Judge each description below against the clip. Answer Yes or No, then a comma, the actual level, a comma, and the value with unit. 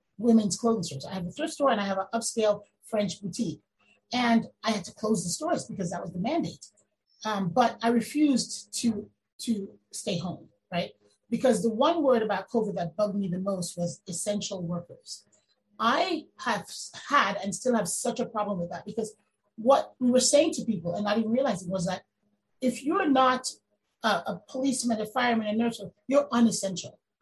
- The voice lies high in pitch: Yes, high, 215 Hz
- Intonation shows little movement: No, average, 4.2 semitones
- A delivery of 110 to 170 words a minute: No, average, 190 wpm